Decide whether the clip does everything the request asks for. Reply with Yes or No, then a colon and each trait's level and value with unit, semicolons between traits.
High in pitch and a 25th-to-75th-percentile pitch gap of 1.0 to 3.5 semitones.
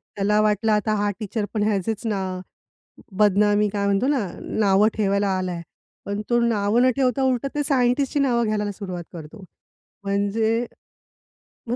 Yes: high, 210 Hz; average, 2.8 semitones